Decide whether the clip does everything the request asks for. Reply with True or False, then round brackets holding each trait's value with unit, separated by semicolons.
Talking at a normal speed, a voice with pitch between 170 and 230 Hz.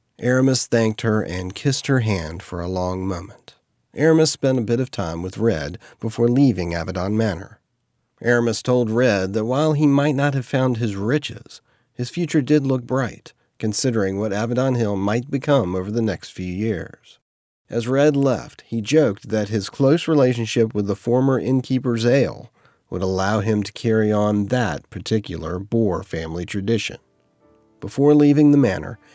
False (165 wpm; 115 Hz)